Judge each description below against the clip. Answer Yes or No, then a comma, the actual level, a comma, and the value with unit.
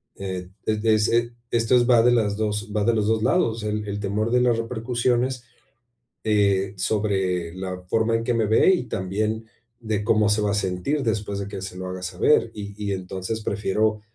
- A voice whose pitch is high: No, low, 105 Hz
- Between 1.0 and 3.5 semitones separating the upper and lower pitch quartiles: Yes, narrow, 2.6 semitones